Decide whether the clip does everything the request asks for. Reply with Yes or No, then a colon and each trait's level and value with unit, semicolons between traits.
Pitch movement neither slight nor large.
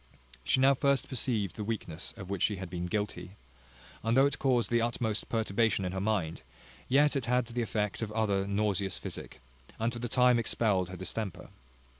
Yes: average, 3.6 semitones